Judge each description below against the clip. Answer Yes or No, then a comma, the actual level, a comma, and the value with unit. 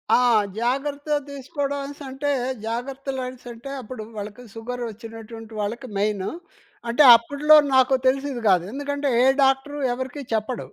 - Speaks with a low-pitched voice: No, very high, 255 Hz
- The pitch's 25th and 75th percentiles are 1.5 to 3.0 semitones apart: No, average, 3.6 semitones